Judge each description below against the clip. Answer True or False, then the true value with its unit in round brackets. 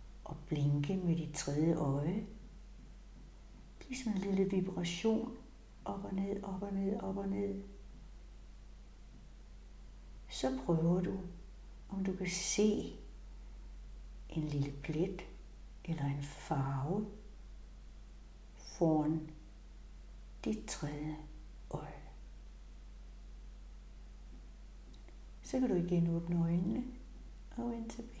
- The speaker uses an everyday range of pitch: False (5.8 semitones)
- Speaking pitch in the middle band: True (170 Hz)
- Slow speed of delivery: True (100 wpm)